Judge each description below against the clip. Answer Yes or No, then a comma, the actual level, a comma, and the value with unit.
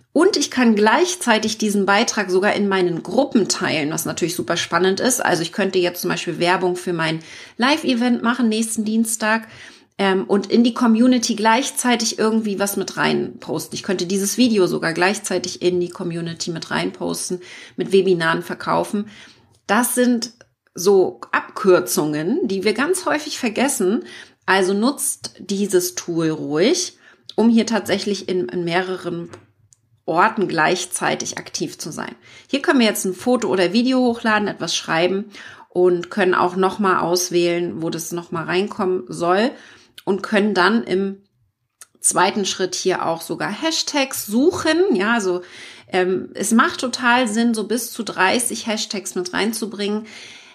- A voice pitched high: Yes, high, 200 Hz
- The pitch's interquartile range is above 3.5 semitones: Yes, average, 4.6 semitones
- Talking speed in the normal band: Yes, average, 150 wpm